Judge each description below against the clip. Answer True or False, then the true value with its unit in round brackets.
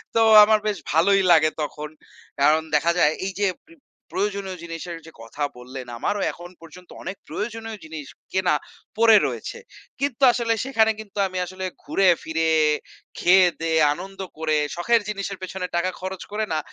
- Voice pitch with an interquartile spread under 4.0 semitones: False (4.3 semitones)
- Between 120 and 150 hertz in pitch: False (185 Hz)